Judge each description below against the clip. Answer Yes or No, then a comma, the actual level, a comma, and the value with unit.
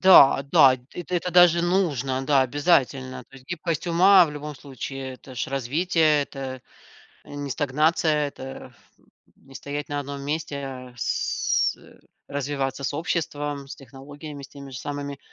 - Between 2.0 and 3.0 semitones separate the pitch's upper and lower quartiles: Yes, narrow, 2.5 semitones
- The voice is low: No, medium, 145 Hz